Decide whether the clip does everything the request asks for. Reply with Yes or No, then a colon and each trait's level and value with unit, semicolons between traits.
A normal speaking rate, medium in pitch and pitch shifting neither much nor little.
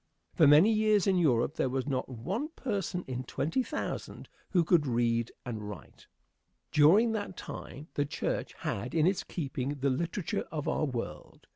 No: average, 165 wpm; medium, 150 Hz; wide, 6.6 semitones